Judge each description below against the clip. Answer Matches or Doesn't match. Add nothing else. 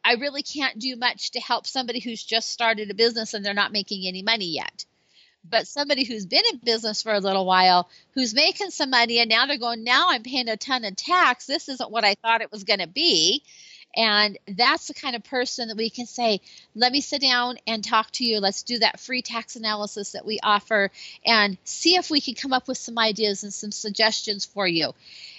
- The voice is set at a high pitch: Matches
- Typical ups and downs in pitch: Matches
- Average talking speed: Doesn't match